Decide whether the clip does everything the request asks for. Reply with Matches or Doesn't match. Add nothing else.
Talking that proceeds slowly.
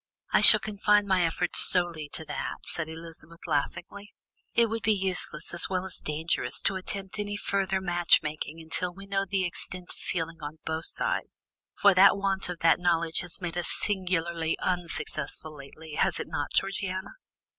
Doesn't match